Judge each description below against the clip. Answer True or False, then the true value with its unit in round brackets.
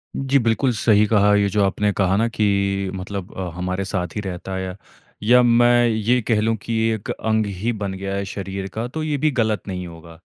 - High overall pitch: False (105 Hz)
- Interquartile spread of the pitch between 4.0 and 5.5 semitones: False (3.0 semitones)